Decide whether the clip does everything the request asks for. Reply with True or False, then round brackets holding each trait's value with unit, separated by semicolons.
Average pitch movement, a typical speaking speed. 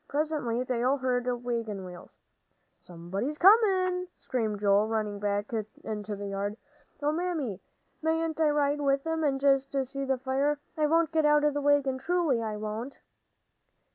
False (5.7 semitones; 160 wpm)